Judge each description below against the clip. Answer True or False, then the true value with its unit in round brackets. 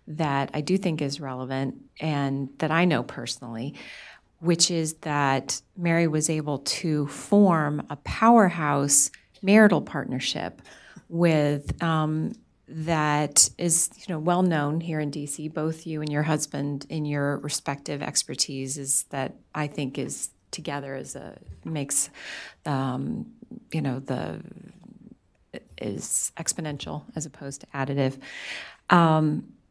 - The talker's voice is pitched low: False (150 Hz)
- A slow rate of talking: True (125 wpm)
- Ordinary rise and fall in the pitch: True (3.2 semitones)